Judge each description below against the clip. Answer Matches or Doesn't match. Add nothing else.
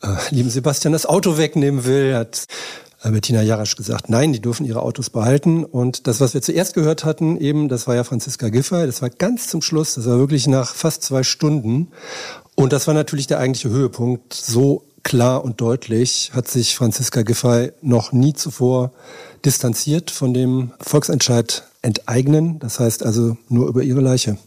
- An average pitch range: Matches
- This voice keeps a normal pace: Matches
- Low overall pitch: Matches